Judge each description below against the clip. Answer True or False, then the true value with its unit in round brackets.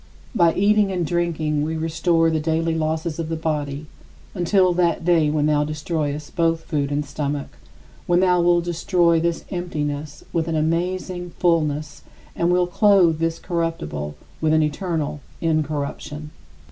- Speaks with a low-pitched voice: False (165 Hz)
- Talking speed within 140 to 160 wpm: True (145 wpm)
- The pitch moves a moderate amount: False (2.3 semitones)